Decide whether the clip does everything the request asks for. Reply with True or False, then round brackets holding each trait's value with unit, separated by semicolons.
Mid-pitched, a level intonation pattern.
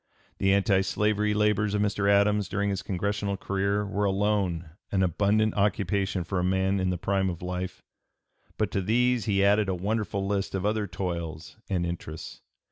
False (100 Hz; 1.8 semitones)